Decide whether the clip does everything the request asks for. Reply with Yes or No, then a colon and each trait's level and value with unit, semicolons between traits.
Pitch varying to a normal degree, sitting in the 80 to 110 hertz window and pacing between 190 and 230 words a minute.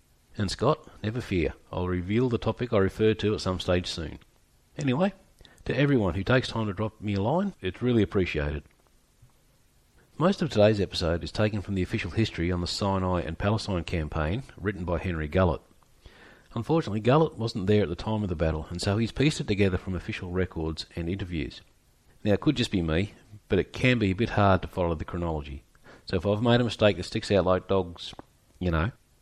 Yes: average, 4.3 semitones; low, 100 Hz; fast, 205 wpm